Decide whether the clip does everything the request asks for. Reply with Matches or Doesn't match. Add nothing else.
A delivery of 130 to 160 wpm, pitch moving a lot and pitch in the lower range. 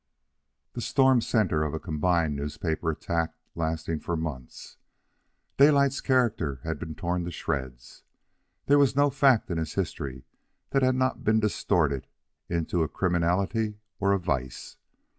Matches